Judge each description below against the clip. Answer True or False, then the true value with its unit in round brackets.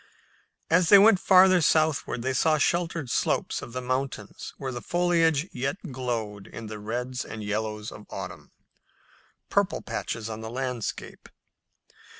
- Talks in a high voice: False (130 Hz)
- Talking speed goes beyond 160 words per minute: False (145 wpm)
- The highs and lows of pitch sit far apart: True (6.5 semitones)